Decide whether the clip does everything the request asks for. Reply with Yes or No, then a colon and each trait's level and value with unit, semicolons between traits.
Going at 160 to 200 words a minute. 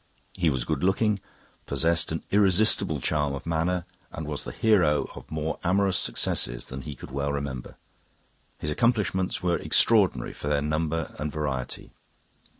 No: average, 150 wpm